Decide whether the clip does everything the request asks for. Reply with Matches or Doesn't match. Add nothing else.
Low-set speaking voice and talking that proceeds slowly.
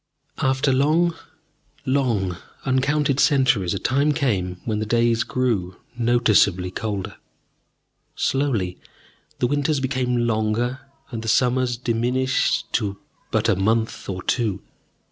Matches